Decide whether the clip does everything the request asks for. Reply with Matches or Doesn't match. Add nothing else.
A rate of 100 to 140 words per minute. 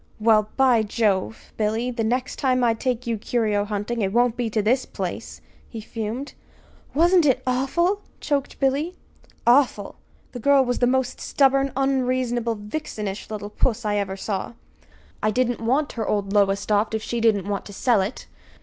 Doesn't match